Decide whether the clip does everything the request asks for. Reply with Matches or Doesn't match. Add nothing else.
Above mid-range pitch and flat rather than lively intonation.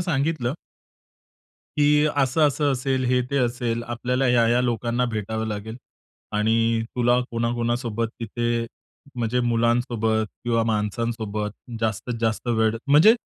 Doesn't match